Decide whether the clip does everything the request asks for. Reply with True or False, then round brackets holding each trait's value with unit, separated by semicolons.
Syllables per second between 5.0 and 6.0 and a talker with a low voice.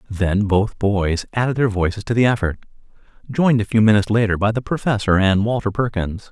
True (5.7 syllables/s; 105 Hz)